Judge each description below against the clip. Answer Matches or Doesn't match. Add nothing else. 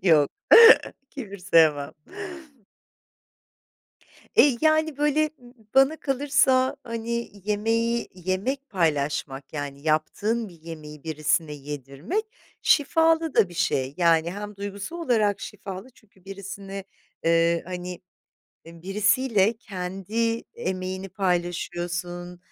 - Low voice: Doesn't match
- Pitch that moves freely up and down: Matches